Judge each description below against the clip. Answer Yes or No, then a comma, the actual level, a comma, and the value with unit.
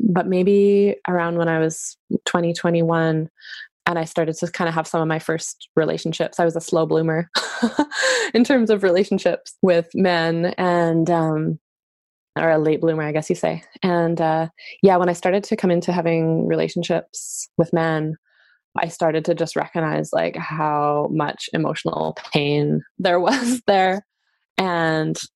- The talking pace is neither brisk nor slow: Yes, average, 160 wpm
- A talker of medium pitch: Yes, medium, 170 Hz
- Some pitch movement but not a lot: No, narrow, 2.3 semitones